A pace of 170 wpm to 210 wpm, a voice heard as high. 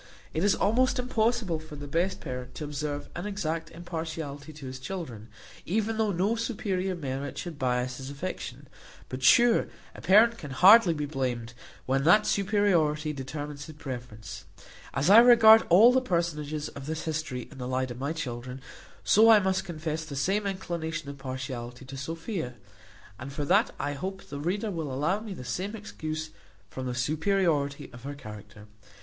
No: average, 175 wpm; medium, 155 Hz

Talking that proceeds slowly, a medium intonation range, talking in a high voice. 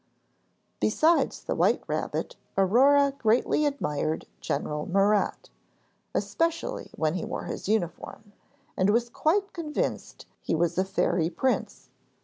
No: slow, 120 wpm; wide, 8.2 semitones; high, 215 Hz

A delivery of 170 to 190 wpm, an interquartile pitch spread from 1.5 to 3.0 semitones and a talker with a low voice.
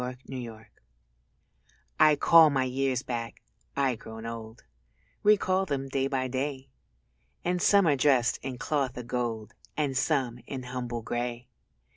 No: average, 145 wpm; average, 2.7 semitones; low, 130 Hz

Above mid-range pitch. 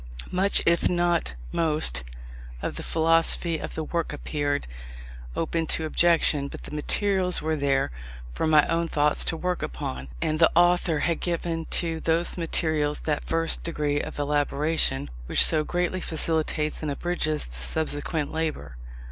No: medium, 160 Hz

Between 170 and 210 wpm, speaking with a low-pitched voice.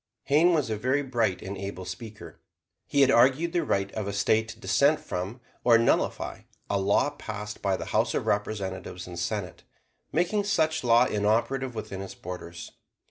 Yes: average, 175 wpm; low, 110 Hz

